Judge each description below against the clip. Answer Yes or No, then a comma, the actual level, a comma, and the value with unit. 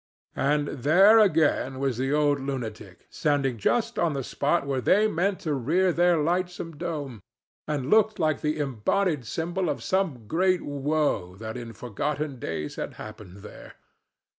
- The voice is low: No, medium, 145 Hz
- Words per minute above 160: No, average, 155 wpm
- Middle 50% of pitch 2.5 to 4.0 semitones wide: No, wide, 5.4 semitones